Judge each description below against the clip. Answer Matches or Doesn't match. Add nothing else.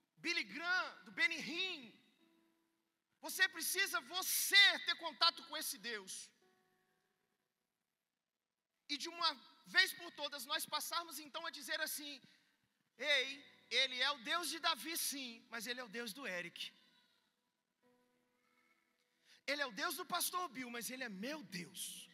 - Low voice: Doesn't match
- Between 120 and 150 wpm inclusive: Matches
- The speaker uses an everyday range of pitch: Doesn't match